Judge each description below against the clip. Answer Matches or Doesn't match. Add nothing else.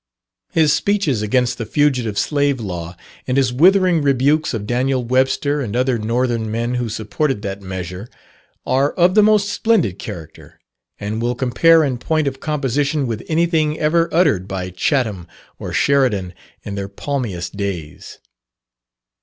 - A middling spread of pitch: Doesn't match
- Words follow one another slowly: Doesn't match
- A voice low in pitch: Matches